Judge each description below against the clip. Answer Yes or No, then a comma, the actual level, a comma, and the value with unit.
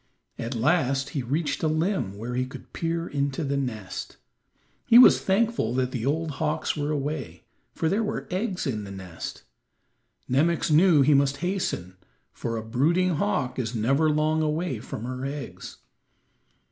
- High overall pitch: No, medium, 140 Hz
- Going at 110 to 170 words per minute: Yes, average, 160 wpm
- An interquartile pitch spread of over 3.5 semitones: Yes, average, 4.8 semitones